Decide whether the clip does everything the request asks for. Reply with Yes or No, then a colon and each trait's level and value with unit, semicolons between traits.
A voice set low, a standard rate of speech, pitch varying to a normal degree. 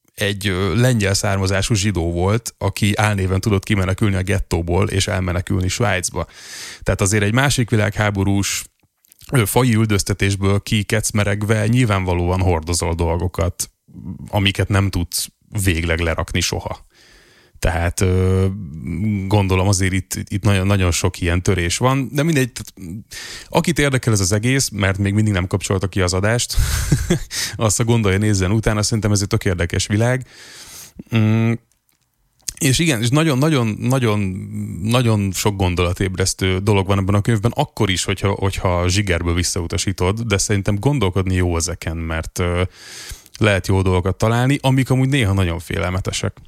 Yes: low, 100 Hz; average, 130 wpm; average, 3.1 semitones